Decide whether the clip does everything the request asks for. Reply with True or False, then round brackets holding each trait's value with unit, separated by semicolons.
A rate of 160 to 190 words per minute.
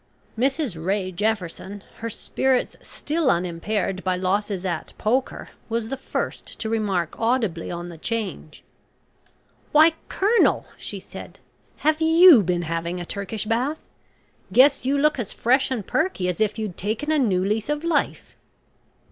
False (150 wpm)